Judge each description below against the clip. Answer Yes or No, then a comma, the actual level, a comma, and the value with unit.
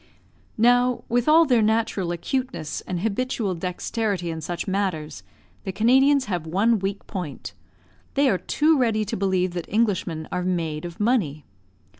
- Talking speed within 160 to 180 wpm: No, average, 150 wpm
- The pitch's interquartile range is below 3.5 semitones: No, wide, 5.4 semitones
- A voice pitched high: Yes, high, 200 Hz